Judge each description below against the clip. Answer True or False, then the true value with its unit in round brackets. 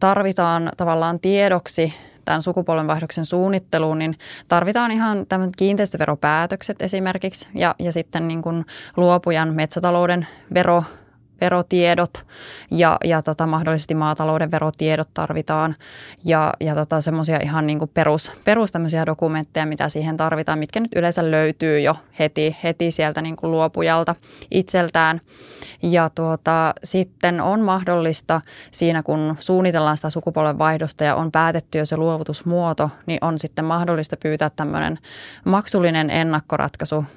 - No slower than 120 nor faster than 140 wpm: True (125 wpm)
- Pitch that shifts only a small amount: True (1.9 semitones)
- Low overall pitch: False (160 Hz)